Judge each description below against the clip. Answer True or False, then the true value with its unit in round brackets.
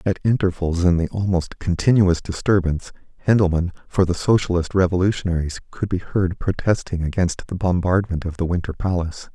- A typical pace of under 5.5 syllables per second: False (5.6 syllables/s)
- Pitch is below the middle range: True (90 Hz)